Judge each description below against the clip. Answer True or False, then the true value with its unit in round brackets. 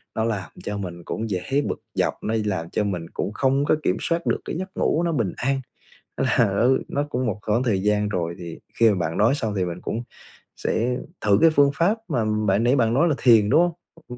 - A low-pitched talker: True (110 Hz)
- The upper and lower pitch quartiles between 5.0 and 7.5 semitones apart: True (5.6 semitones)